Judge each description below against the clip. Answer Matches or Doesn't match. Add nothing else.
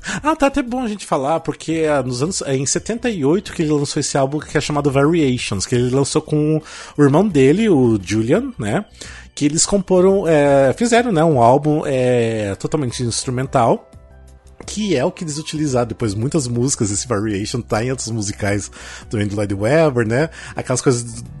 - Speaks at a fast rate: Matches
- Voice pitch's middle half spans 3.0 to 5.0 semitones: Doesn't match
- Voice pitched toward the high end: Doesn't match